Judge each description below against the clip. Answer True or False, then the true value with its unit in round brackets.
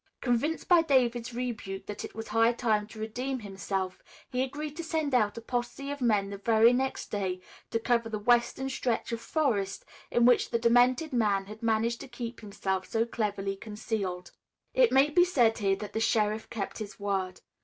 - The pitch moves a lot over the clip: False (3.4 semitones)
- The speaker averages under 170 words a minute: False (190 wpm)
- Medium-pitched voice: False (230 Hz)